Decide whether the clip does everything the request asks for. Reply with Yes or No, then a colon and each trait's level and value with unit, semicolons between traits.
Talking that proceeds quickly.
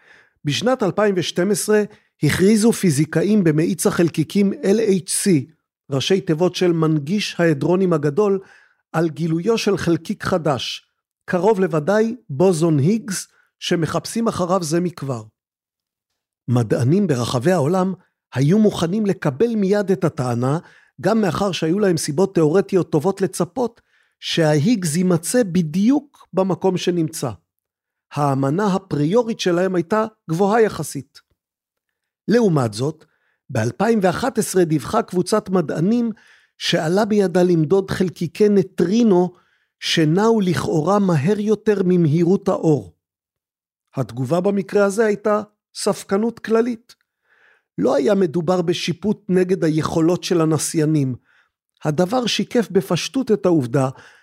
No: slow, 100 wpm